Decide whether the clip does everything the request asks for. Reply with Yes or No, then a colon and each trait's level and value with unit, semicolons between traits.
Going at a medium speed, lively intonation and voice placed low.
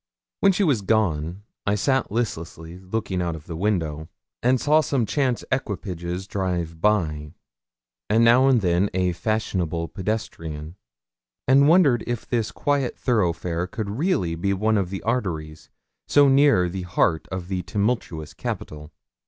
Yes: average, 145 wpm; wide, 5.9 semitones; very low, 95 Hz